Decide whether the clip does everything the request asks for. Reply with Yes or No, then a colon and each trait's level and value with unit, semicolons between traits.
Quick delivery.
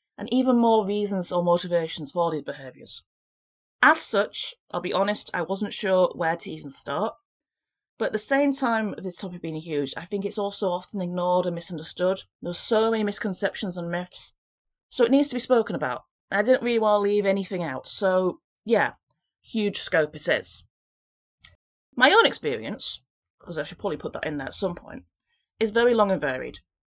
No: average, 190 wpm